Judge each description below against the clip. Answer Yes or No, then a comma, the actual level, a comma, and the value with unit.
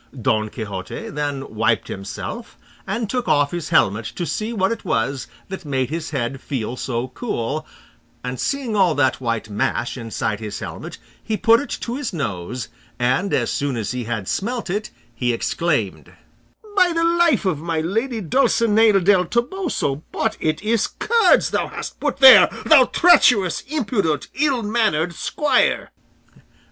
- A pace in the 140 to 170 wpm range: Yes, average, 155 wpm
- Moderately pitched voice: Yes, medium, 165 Hz